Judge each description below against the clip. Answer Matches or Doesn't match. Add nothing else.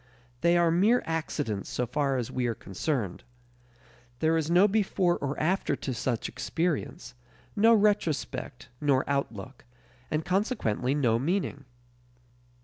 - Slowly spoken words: Matches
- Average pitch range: Doesn't match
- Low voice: Doesn't match